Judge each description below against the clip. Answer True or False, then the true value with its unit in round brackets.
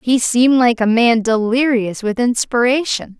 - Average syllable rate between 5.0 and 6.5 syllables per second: False (4.5 syllables/s)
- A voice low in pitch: False (240 Hz)